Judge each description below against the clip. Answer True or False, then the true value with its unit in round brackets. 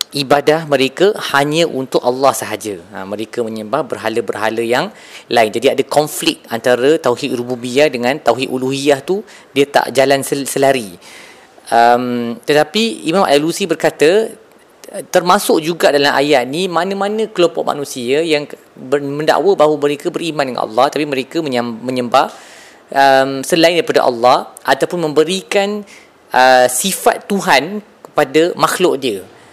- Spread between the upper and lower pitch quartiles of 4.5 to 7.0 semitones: True (4.9 semitones)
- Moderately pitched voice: True (145 Hz)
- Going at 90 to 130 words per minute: True (125 wpm)